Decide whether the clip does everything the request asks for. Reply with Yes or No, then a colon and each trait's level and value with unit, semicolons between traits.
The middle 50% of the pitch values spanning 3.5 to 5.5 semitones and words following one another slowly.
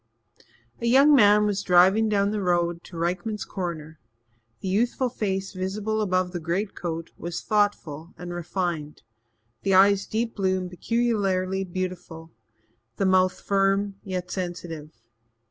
No: average, 2.8 semitones; slow, 130 wpm